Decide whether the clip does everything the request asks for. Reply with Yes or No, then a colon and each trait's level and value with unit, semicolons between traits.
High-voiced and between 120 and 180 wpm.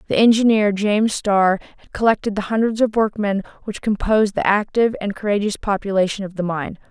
Yes: high, 205 Hz; average, 175 wpm